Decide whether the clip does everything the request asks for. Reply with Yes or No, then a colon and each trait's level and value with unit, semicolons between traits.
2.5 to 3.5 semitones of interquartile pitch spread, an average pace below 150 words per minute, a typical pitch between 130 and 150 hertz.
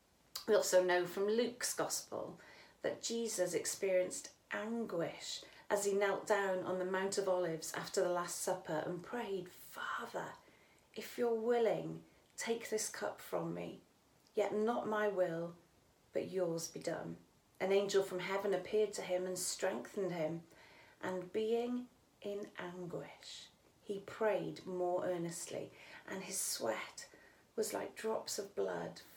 No: average, 3.1 semitones; average, 140 wpm; medium, 185 Hz